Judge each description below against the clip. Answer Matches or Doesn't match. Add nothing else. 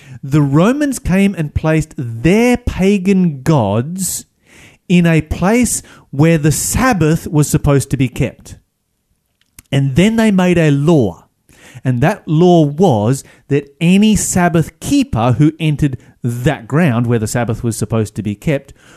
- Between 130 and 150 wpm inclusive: Matches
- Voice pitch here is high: Doesn't match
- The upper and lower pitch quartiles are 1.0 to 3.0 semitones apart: Doesn't match